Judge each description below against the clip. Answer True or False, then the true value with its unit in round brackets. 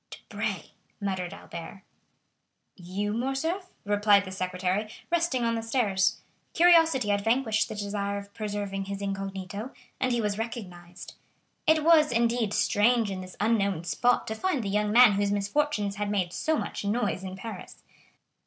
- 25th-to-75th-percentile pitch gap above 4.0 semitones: False (3.4 semitones)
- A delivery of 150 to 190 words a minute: True (155 wpm)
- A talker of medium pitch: False (205 Hz)